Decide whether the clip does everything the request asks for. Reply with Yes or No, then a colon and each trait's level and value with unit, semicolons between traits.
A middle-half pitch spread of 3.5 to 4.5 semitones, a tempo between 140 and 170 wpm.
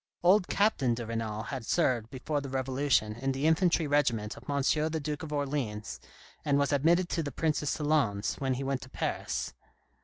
No: average, 3.8 semitones; average, 185 wpm